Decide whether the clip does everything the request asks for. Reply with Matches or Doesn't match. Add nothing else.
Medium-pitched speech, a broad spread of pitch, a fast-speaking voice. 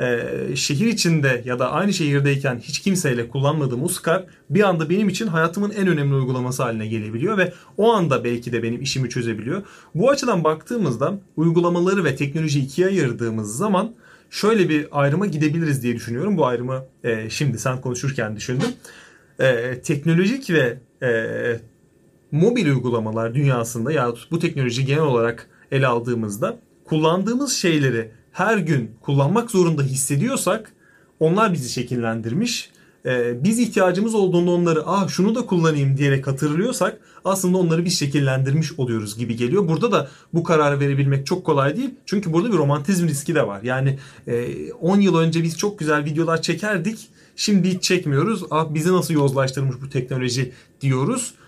Matches